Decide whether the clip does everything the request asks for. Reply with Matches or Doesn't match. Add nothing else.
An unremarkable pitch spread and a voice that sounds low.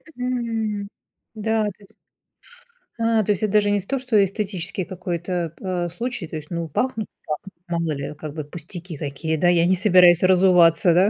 Doesn't match